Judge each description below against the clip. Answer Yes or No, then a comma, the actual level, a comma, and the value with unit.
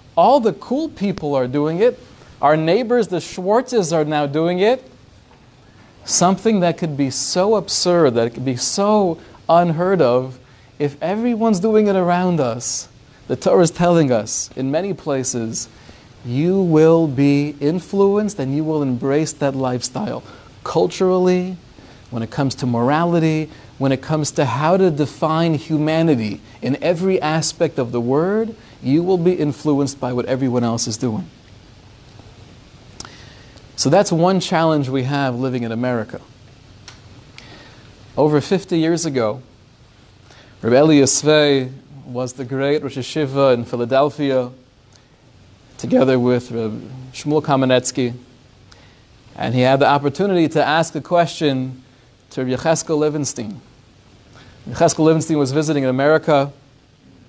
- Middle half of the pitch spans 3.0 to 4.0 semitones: No, average, 4.7 semitones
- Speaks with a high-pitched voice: No, medium, 140 Hz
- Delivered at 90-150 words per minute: Yes, slow, 135 wpm